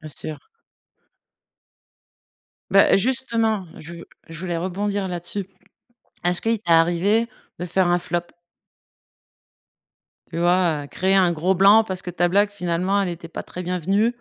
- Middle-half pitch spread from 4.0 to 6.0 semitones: No, average, 2.7 semitones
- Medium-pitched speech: Yes, medium, 180 Hz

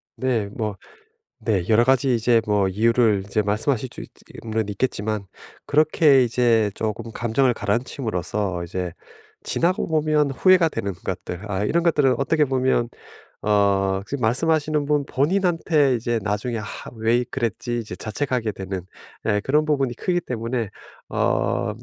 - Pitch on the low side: Yes, low, 120 Hz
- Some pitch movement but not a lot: Yes, average, 4.9 semitones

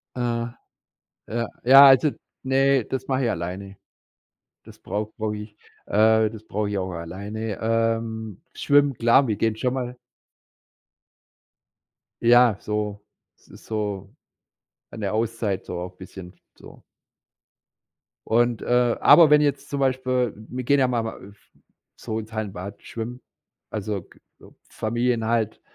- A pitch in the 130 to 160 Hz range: No, low, 110 Hz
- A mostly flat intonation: No, average, 3.0 semitones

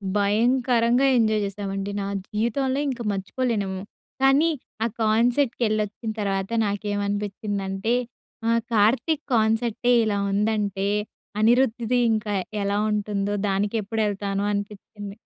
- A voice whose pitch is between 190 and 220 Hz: Yes, high, 210 Hz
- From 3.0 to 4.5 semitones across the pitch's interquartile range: No, narrow, 2.6 semitones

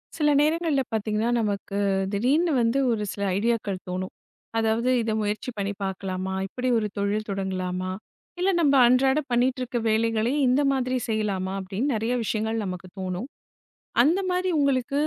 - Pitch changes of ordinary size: Yes, average, 4.5 semitones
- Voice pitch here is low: No, high, 220 Hz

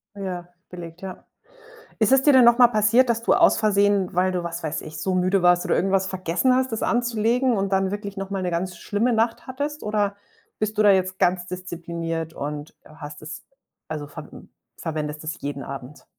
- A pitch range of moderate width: Yes, average, 4.2 semitones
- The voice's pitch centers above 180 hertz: Yes, high, 190 Hz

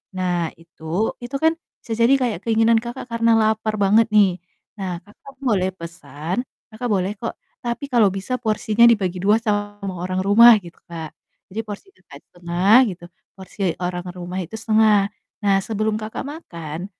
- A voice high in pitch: Yes, high, 205 Hz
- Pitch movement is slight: No, average, 4.0 semitones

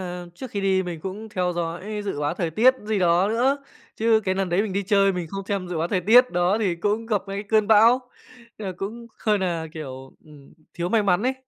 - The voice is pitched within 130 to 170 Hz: No, high, 195 Hz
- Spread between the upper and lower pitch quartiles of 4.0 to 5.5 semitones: No, average, 3.6 semitones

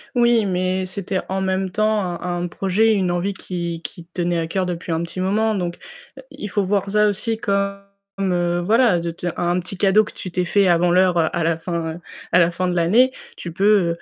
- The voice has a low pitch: No, medium, 185 Hz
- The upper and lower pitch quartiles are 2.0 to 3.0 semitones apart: Yes, narrow, 2.5 semitones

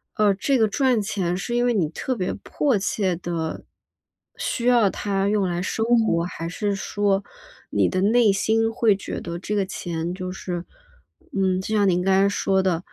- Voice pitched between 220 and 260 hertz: No, high, 195 Hz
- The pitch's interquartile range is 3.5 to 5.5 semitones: No, average, 3.1 semitones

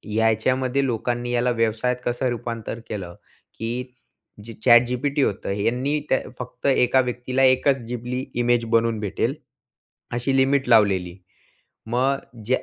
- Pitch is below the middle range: Yes, low, 120 Hz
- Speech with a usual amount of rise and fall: No, narrow, 2.1 semitones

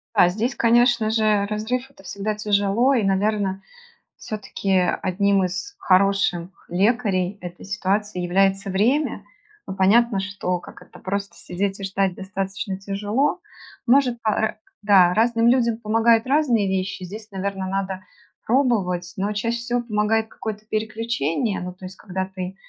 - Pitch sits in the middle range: No, high, 200 Hz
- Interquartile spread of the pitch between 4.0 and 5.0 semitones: No, average, 3.0 semitones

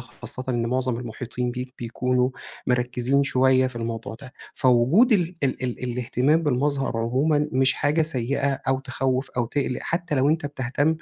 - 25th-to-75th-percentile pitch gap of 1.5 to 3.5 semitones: Yes, narrow, 2.5 semitones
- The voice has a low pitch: Yes, low, 130 Hz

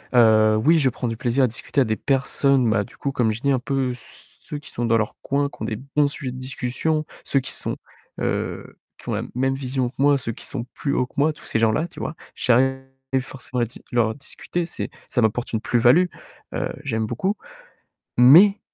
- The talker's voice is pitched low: Yes, low, 130 Hz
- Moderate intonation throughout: Yes, average, 3.2 semitones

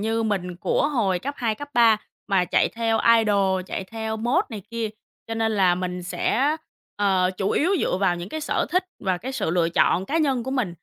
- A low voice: No, high, 220 Hz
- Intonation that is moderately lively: Yes, average, 4.5 semitones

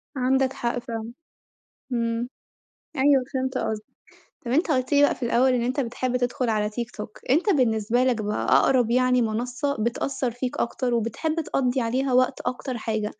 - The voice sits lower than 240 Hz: No, high, 245 Hz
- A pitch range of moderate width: No, narrow, 2.1 semitones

